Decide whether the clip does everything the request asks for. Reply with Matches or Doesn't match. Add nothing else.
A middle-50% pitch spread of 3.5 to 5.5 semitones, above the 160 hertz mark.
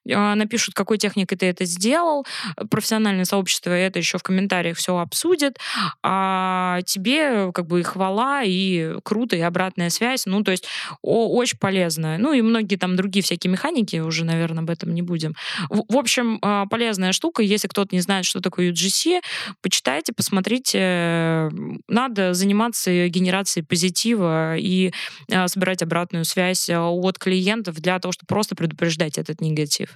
Doesn't match